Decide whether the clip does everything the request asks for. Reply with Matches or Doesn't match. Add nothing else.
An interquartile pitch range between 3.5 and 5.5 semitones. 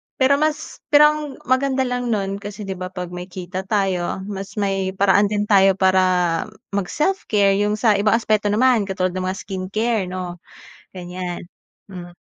Doesn't match